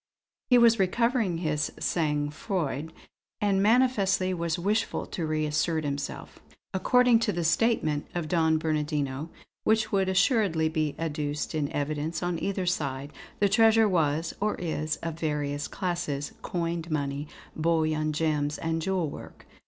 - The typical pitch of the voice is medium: Yes, medium, 165 Hz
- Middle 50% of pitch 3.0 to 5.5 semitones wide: Yes, average, 4.2 semitones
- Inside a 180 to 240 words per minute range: No, slow, 135 wpm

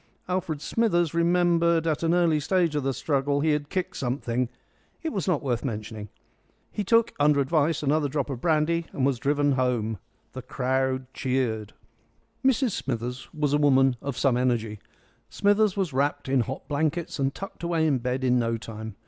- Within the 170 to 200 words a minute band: Yes, average, 180 wpm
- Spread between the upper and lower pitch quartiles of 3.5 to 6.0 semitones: Yes, average, 4.6 semitones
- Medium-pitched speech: Yes, medium, 145 Hz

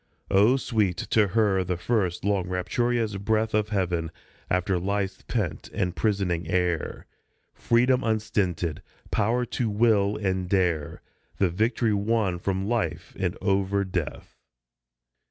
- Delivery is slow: Yes, slow, 125 wpm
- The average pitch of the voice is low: Yes, low, 100 Hz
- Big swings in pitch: No, average, 3.3 semitones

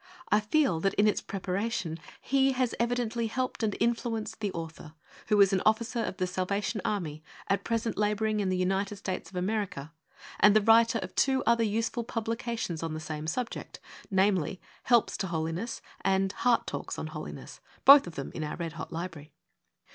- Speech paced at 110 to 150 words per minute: No, average, 185 wpm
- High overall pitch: Yes, high, 205 Hz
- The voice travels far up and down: No, average, 4.1 semitones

